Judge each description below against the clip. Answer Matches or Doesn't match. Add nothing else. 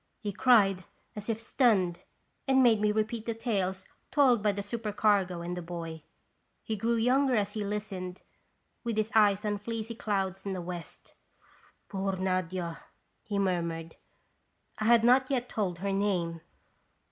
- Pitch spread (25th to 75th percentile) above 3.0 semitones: Matches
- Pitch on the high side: Matches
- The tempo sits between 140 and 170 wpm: Matches